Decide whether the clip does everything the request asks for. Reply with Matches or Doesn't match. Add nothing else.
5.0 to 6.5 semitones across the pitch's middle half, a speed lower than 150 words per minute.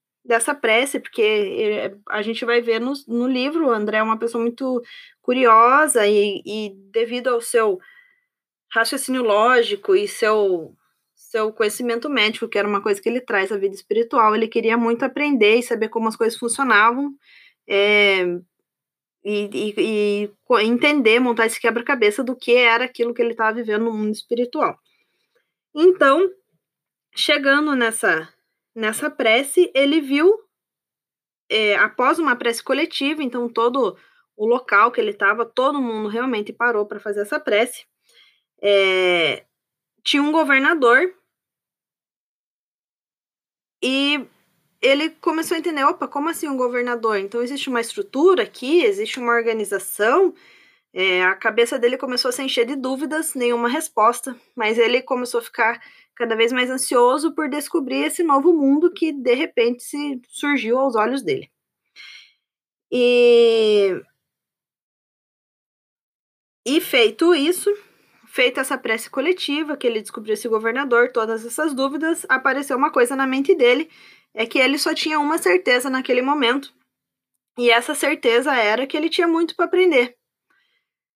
Matches